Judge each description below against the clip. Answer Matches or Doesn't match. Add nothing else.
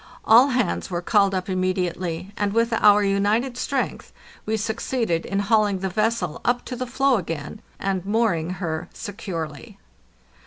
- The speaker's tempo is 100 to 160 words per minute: Matches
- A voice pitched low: Doesn't match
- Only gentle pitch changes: Doesn't match